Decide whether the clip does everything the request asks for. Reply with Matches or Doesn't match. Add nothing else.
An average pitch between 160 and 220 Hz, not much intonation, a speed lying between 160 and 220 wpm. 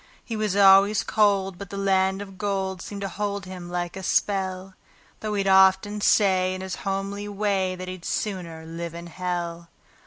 Matches